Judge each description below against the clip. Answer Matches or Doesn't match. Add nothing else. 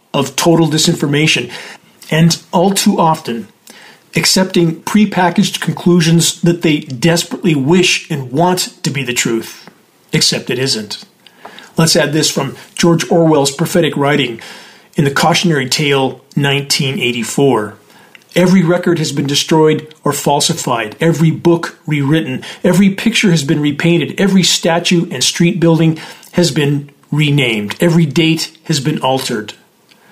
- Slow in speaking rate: Matches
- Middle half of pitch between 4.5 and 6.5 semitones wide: Doesn't match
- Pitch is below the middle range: Doesn't match